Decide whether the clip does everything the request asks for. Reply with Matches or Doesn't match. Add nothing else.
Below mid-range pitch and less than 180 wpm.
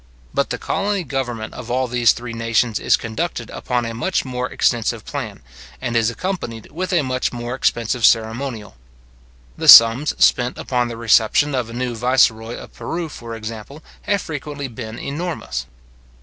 Matches